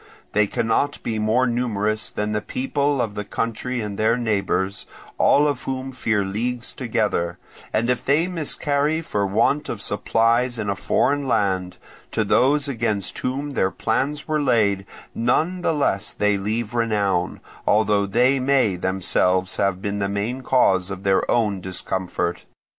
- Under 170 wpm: Yes, average, 155 wpm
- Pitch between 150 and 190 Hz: No, low, 110 Hz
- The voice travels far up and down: No, average, 4.5 semitones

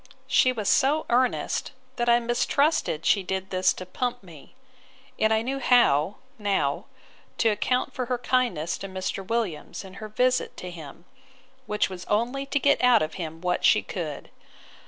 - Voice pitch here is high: Yes, high, 215 Hz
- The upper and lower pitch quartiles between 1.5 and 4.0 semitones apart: No, average, 5.3 semitones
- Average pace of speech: Yes, average, 170 wpm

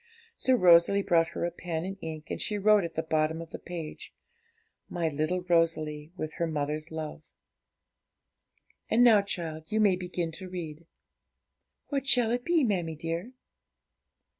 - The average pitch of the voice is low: No, medium, 170 Hz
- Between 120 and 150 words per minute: No, average, 160 wpm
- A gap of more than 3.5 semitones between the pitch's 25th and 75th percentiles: Yes, average, 3.9 semitones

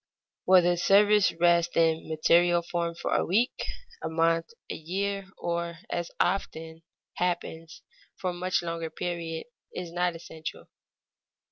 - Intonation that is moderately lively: No, narrow, 1.4 semitones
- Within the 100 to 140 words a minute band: Yes, slow, 135 wpm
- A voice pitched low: No, medium, 170 Hz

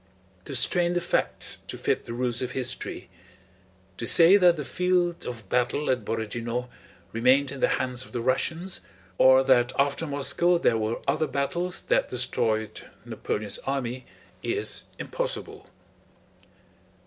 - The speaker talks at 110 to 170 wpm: Yes, average, 140 wpm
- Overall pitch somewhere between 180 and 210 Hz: No, low, 130 Hz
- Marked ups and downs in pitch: Yes, wide, 6.0 semitones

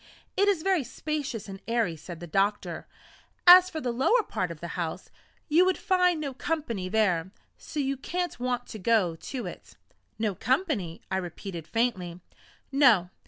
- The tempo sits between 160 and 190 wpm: Yes, average, 165 wpm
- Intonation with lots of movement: Yes, wide, 8.8 semitones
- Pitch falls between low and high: No, high, 235 Hz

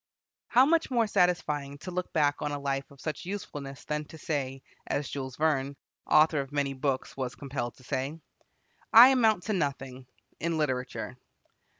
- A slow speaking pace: No, average, 170 wpm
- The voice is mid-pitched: Yes, medium, 145 Hz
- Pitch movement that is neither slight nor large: Yes, average, 3.9 semitones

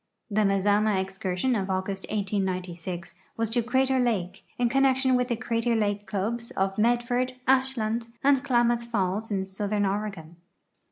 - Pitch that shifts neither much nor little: Yes, average, 3.9 semitones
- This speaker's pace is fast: No, average, 150 wpm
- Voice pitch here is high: Yes, high, 215 Hz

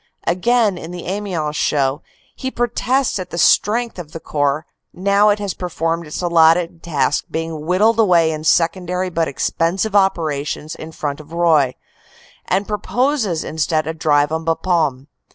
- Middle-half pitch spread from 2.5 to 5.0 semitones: Yes, average, 3.8 semitones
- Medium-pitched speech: Yes, medium, 170 Hz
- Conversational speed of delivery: Yes, average, 150 wpm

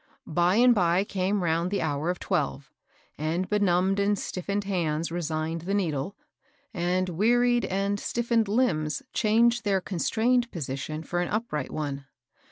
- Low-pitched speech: No, medium, 185 Hz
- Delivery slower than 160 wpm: Yes, average, 150 wpm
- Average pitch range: Yes, average, 4.4 semitones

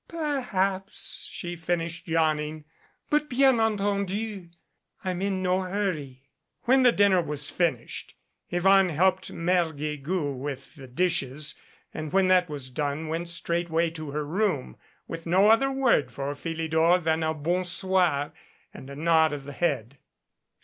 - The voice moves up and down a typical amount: Yes, average, 4.0 semitones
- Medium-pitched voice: Yes, medium, 170 Hz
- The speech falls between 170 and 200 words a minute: No, average, 145 wpm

